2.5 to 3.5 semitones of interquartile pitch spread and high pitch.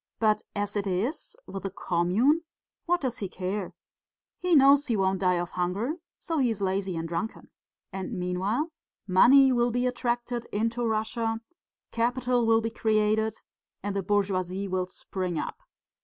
No: average, 4.3 semitones; high, 215 Hz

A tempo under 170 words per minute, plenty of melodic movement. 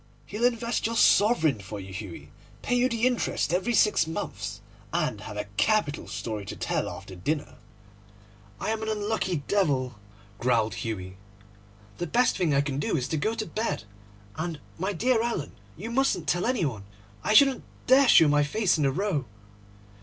No: average, 175 wpm; wide, 8.7 semitones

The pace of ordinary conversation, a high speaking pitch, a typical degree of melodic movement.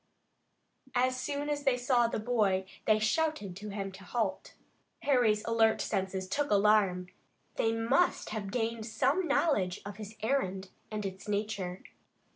Yes: average, 145 wpm; high, 215 Hz; average, 4.1 semitones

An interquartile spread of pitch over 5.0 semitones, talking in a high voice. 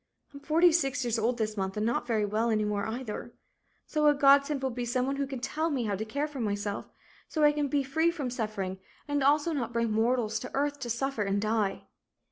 No: average, 4.6 semitones; very high, 250 Hz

